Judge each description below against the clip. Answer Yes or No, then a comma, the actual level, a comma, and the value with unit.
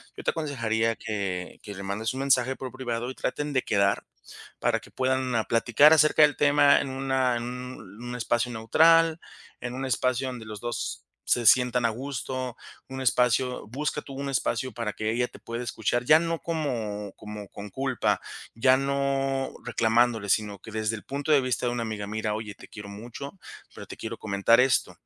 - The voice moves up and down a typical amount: Yes, average, 3.2 semitones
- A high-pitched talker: No, low, 125 Hz